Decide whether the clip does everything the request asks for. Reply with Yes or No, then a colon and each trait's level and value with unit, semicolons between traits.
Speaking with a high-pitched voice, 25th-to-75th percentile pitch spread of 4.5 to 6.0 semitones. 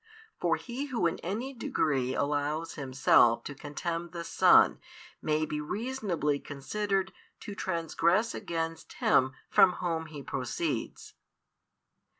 No: medium, 165 Hz; average, 4.8 semitones